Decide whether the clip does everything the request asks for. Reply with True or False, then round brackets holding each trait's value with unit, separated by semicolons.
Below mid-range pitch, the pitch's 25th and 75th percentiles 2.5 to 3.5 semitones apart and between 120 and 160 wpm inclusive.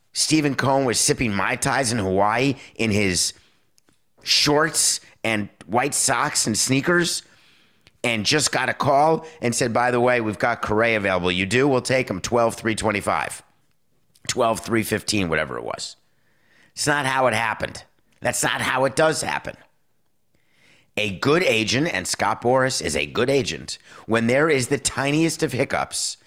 False (125 Hz; 4.3 semitones; 155 wpm)